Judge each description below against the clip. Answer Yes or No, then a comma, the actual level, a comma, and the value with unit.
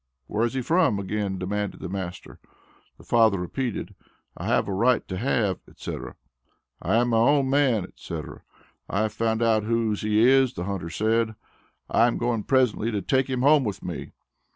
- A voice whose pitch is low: Yes, low, 110 Hz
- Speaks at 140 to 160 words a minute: No, average, 180 wpm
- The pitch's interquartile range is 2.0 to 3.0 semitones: No, average, 3.7 semitones